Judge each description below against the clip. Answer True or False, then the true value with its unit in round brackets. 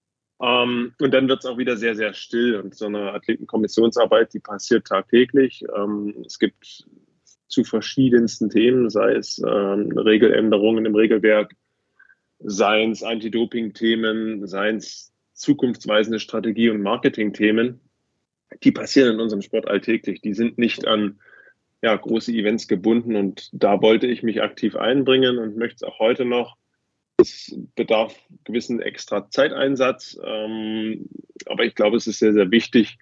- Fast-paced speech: False (140 wpm)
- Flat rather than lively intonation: True (2.2 semitones)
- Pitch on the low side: True (115 Hz)